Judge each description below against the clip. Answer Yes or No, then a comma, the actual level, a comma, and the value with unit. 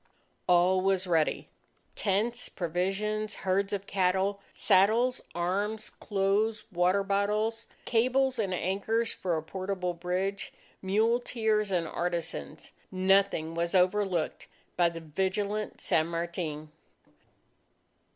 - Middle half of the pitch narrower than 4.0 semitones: Yes, average, 3.0 semitones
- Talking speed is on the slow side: Yes, slow, 100 wpm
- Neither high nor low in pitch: No, high, 195 Hz